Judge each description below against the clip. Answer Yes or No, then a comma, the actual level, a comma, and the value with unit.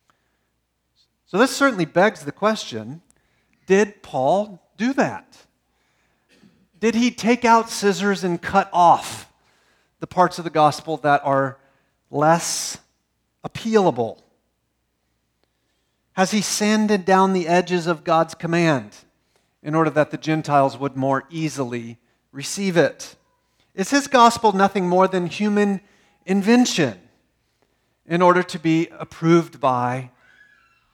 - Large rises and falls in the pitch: Yes, wide, 6.3 semitones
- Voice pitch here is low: No, medium, 170 Hz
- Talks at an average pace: No, slow, 115 wpm